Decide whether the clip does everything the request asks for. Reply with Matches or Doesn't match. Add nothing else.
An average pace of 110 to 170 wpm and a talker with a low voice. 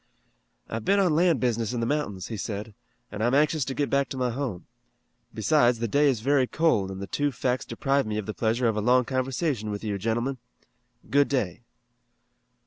Doesn't match